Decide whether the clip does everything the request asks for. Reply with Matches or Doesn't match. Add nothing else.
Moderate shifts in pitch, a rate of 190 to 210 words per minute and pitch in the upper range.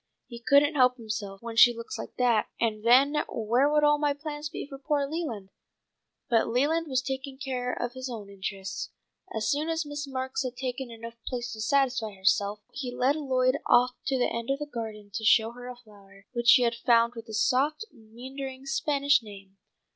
Matches